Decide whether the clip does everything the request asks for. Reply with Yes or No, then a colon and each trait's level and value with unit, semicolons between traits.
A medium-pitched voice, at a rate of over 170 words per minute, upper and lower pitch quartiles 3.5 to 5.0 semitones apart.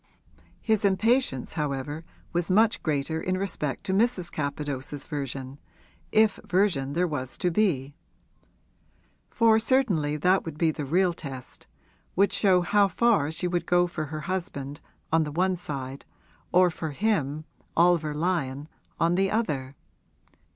No: medium, 165 Hz; average, 140 wpm; average, 4.7 semitones